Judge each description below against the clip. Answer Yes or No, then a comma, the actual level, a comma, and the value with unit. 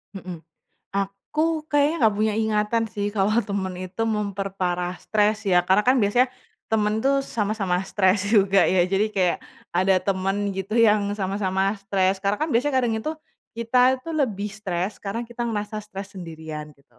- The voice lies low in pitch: No, high, 200 Hz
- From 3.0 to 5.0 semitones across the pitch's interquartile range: No, narrow, 2.4 semitones